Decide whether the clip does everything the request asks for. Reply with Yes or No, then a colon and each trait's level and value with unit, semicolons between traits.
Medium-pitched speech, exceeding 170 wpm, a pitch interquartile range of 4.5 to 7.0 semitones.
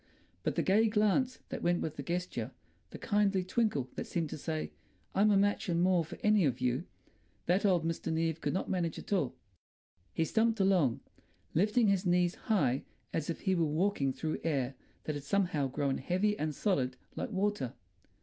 Yes: medium, 175 Hz; average, 185 wpm; average, 5.2 semitones